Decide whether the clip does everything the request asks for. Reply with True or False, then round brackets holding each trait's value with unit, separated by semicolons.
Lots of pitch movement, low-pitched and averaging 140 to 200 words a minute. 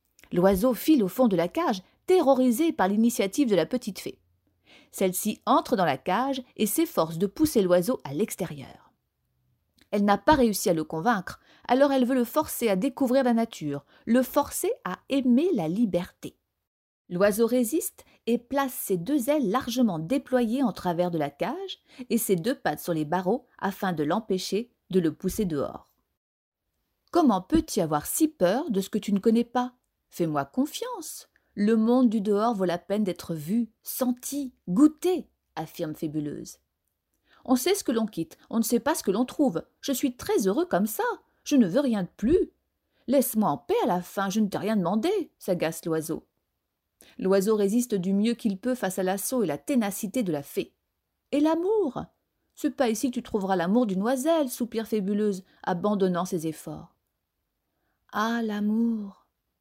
False (6.0 semitones; 225 Hz; 175 wpm)